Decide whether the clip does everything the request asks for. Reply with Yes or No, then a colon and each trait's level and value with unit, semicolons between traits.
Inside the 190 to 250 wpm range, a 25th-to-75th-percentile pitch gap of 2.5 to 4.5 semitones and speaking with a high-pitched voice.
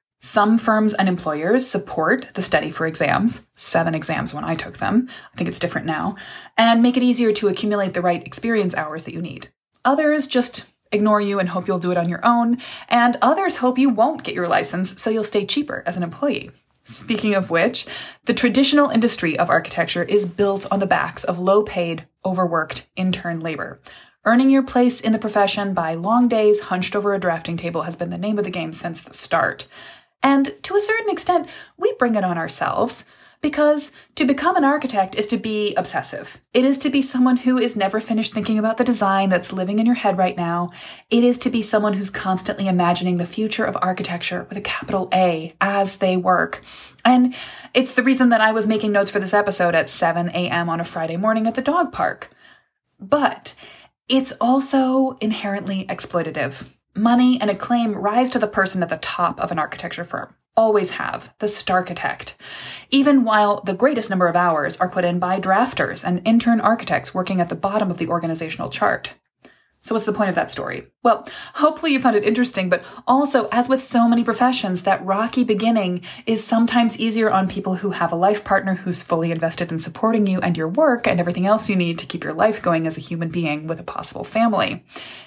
No: fast, 205 wpm; average, 5.0 semitones; high, 205 Hz